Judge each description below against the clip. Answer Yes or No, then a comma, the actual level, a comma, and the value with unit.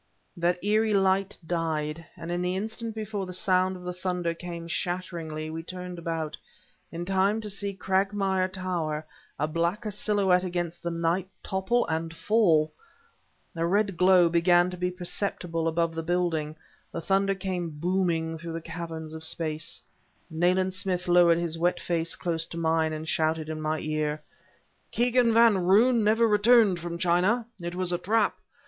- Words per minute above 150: Yes, average, 165 wpm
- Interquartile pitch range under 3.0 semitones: Yes, narrow, 2.6 semitones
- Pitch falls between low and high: Yes, medium, 175 Hz